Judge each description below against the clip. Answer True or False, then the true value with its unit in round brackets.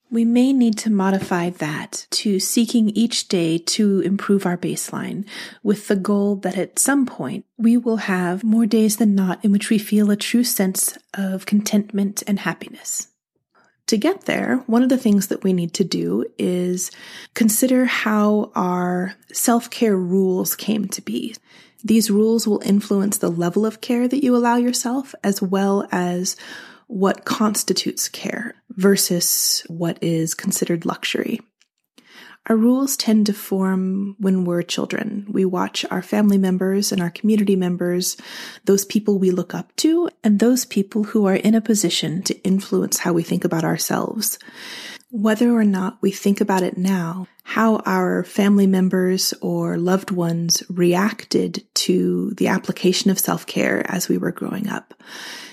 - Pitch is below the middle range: False (200 Hz)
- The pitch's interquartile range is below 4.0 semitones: True (3.2 semitones)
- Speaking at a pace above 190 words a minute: False (160 wpm)